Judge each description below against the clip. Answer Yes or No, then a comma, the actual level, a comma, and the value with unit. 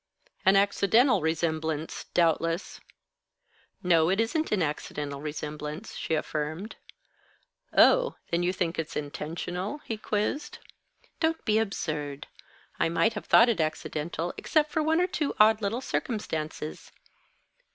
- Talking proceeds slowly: Yes, slow, 125 wpm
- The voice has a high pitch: No, medium, 175 Hz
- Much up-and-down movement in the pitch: Yes, wide, 6.0 semitones